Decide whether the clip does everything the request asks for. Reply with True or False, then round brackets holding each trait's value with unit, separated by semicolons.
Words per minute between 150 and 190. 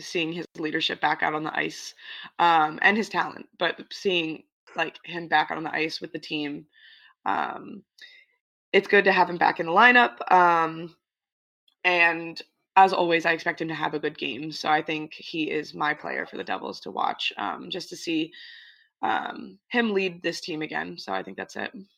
False (200 wpm)